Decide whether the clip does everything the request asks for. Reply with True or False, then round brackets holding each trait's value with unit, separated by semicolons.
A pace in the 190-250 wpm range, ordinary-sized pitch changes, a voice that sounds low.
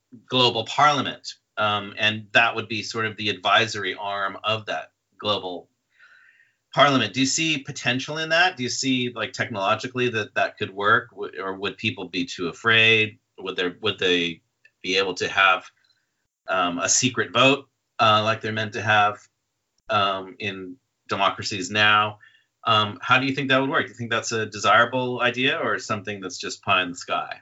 False (180 wpm; 3.3 semitones; 110 Hz)